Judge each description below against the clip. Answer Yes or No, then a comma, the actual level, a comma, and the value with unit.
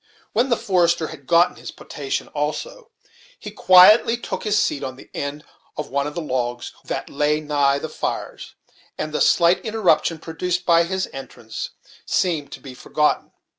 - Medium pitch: Yes, medium, 160 Hz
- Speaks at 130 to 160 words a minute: No, average, 170 wpm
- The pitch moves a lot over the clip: No, average, 4.2 semitones